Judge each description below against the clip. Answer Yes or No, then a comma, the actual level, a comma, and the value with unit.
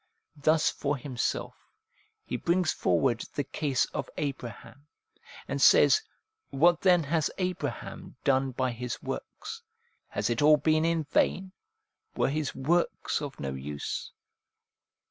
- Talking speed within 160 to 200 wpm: No, slow, 135 wpm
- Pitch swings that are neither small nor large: Yes, average, 4.1 semitones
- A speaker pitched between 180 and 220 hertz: No, medium, 145 Hz